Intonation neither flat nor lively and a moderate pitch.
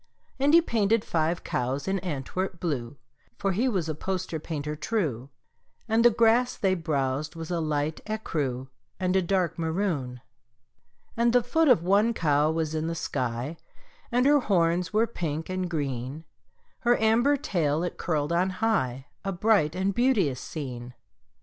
No: wide, 6.2 semitones; medium, 175 Hz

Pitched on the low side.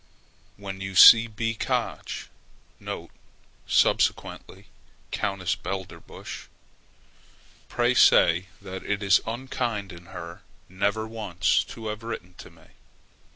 Yes: low, 100 Hz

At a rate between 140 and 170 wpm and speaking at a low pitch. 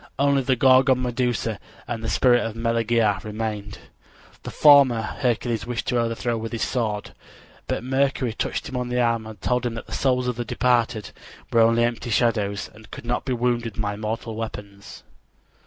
No: average, 185 wpm; low, 115 Hz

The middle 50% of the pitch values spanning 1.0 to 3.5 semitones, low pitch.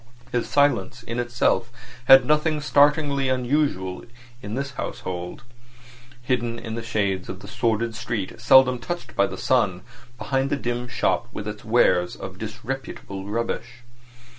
No: average, 4.2 semitones; low, 120 Hz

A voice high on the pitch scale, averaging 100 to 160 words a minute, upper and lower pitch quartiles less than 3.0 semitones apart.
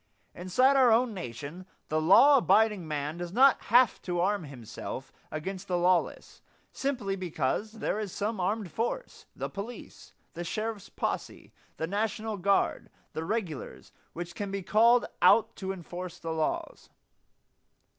No: high, 195 Hz; average, 145 wpm; average, 4.3 semitones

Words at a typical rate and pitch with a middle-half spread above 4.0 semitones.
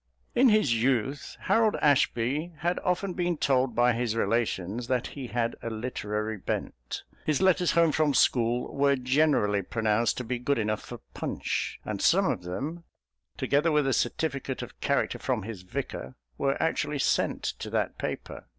Yes: average, 165 wpm; average, 4.7 semitones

